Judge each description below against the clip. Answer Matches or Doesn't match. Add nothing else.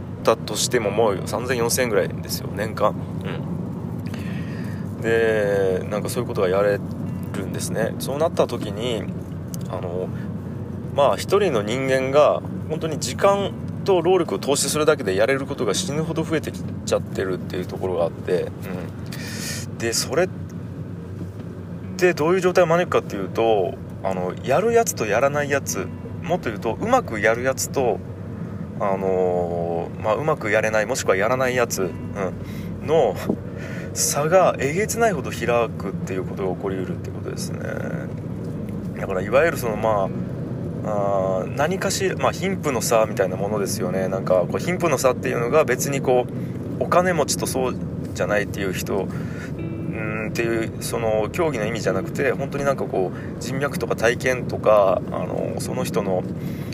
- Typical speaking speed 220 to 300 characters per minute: Doesn't match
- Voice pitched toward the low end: Matches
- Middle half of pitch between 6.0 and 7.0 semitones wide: Matches